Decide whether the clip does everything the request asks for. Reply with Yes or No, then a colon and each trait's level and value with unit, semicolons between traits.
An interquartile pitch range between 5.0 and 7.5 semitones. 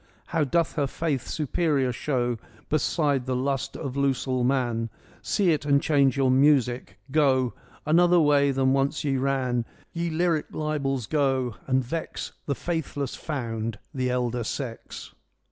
No: average, 3.1 semitones